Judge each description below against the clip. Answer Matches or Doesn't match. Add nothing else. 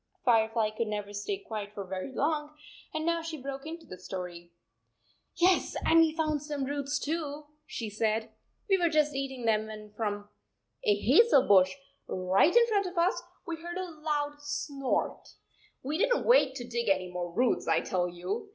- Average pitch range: Doesn't match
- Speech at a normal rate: Matches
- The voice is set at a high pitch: Matches